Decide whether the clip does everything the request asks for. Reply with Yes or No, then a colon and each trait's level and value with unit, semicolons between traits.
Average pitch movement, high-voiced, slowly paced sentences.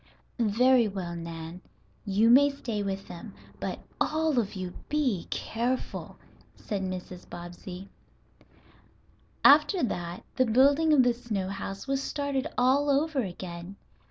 No: wide, 6.6 semitones; high, 225 Hz; slow, 130 wpm